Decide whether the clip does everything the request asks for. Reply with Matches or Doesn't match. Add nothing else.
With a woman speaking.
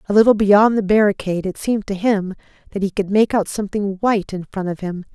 Matches